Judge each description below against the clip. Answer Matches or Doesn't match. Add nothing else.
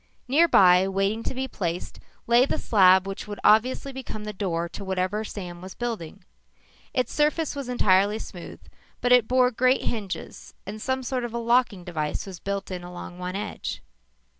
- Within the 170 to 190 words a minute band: Matches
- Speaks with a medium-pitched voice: Doesn't match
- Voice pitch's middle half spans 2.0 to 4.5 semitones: Doesn't match